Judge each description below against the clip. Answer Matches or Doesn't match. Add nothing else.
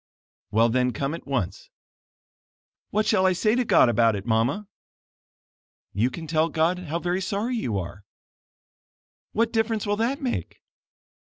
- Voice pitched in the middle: Matches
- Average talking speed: Matches